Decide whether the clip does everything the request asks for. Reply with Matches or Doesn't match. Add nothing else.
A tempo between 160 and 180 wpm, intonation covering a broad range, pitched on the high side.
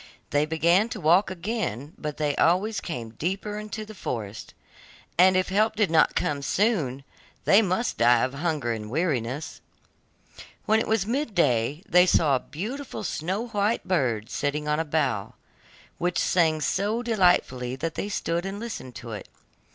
Doesn't match